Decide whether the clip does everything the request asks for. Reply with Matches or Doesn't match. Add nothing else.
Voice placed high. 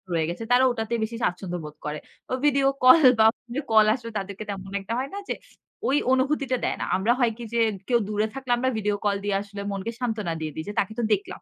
Matches